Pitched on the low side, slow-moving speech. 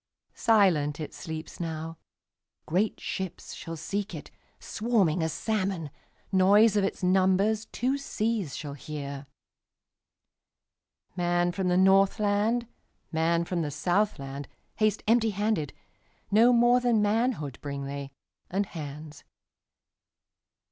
No: medium, 185 Hz; slow, 85 wpm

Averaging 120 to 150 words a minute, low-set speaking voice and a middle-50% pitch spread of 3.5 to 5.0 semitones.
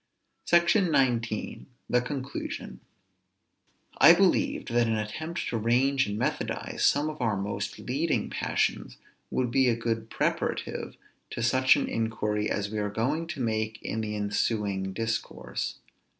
Yes: average, 140 wpm; low, 115 Hz; average, 4.2 semitones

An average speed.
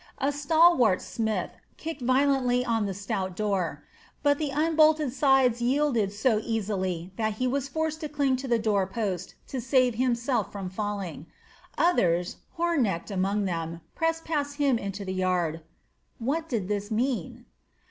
Yes: average, 150 wpm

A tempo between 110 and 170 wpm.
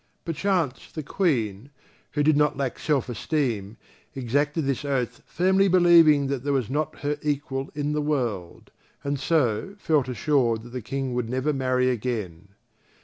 Yes: average, 155 wpm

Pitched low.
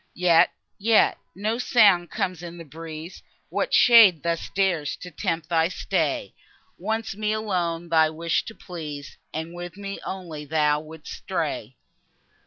No: medium, 170 Hz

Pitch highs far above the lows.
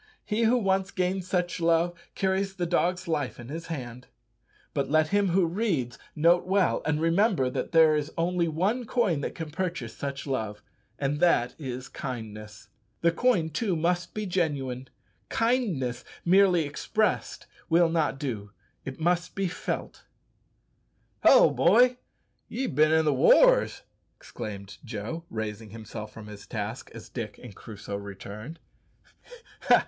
Yes: wide, 6.7 semitones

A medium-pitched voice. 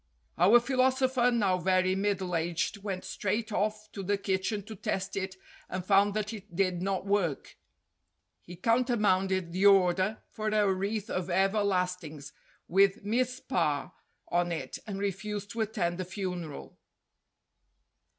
No: high, 195 Hz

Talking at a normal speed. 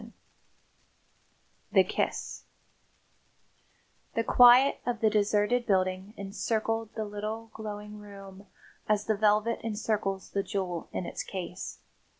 No: slow, 115 wpm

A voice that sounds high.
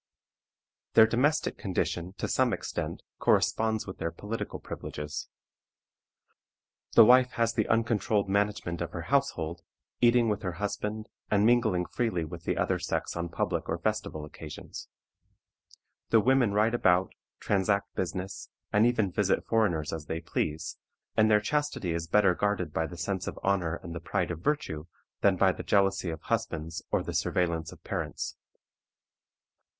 No: very low, 95 Hz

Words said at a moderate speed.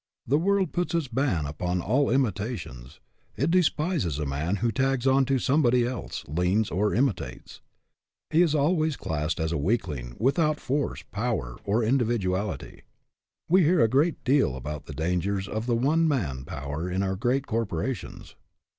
Yes: average, 165 wpm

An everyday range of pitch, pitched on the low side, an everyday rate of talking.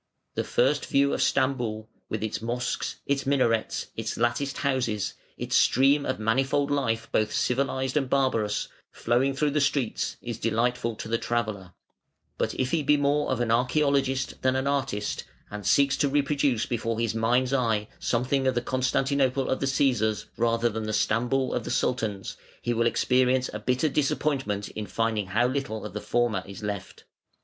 Yes: average, 3.4 semitones; low, 125 Hz; average, 175 wpm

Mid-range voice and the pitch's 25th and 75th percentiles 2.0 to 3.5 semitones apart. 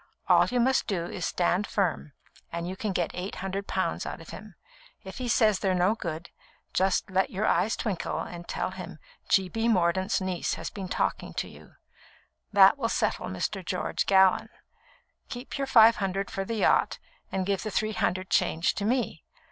No: high, 195 Hz; average, 3.0 semitones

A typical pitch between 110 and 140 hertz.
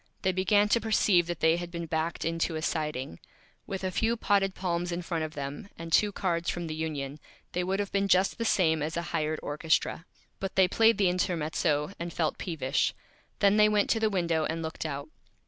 No: medium, 170 Hz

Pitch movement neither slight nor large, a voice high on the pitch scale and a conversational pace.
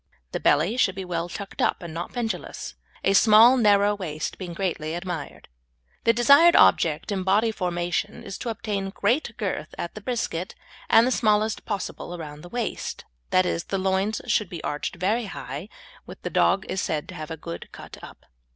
Yes: average, 4.1 semitones; high, 195 Hz; average, 190 wpm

